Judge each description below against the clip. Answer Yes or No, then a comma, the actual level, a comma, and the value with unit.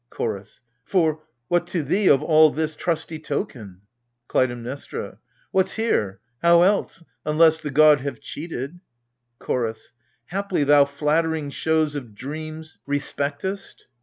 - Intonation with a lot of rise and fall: No, average, 3.2 semitones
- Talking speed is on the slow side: Yes, slow, 125 wpm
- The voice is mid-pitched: Yes, medium, 155 Hz